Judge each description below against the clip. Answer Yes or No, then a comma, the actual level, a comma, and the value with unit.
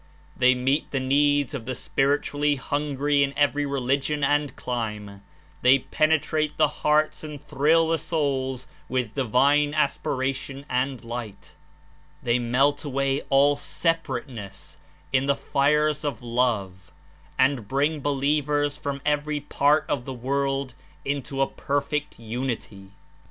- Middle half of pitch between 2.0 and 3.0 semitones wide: Yes, narrow, 2.4 semitones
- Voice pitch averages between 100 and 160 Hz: Yes, medium, 140 Hz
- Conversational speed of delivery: No, slow, 125 wpm